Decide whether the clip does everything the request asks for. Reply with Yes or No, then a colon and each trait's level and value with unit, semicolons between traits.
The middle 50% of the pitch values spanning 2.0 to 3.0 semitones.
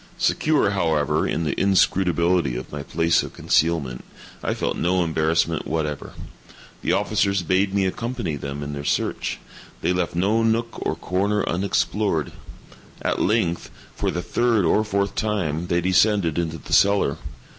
No: average, 3.8 semitones